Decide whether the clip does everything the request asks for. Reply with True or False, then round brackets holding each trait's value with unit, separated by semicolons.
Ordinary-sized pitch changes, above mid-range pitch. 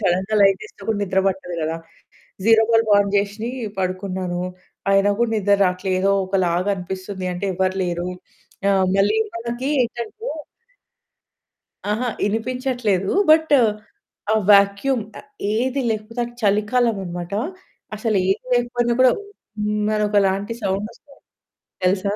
True (3.2 semitones; 200 Hz)